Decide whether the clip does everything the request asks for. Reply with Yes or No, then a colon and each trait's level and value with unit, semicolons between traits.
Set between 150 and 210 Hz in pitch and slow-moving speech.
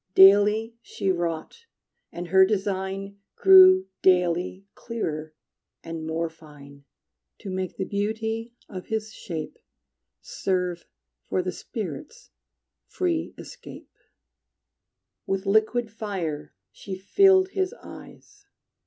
Yes: high, 190 Hz; slow, 100 wpm